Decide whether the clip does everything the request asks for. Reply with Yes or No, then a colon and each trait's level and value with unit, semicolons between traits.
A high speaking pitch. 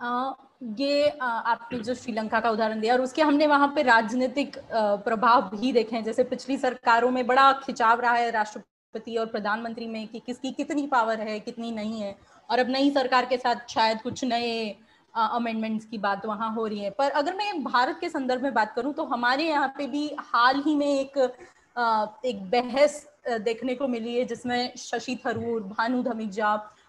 Yes: high, 245 Hz